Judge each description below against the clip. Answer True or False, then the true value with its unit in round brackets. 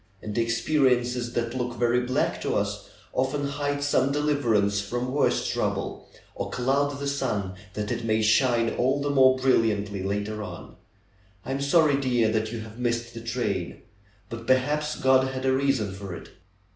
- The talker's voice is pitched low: True (125 Hz)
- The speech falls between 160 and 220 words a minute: True (170 wpm)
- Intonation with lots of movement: False (3.7 semitones)